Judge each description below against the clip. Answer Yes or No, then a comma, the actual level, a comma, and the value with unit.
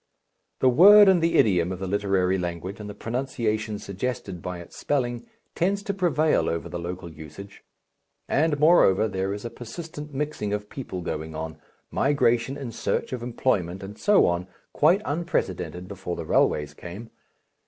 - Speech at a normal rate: Yes, average, 165 wpm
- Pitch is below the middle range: Yes, low, 105 Hz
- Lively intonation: Yes, wide, 7.8 semitones